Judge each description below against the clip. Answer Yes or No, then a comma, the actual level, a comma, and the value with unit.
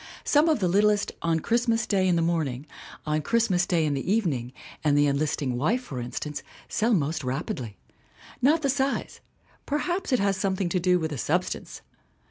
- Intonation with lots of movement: Yes, wide, 7.4 semitones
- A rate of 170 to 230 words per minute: Yes, average, 195 wpm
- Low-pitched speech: No, medium, 180 Hz